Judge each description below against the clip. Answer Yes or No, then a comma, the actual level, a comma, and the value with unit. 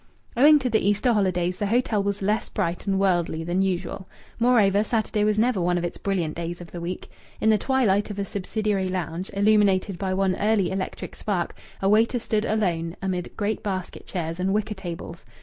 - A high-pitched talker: Yes, high, 195 Hz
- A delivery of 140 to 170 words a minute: No, average, 195 wpm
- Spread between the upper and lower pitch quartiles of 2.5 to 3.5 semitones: Yes, average, 2.9 semitones